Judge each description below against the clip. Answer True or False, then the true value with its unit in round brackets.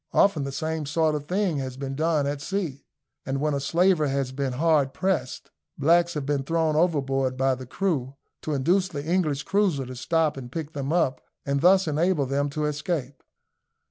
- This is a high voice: False (150 Hz)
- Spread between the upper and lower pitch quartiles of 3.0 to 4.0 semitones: True (3.5 semitones)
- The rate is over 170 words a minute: True (190 wpm)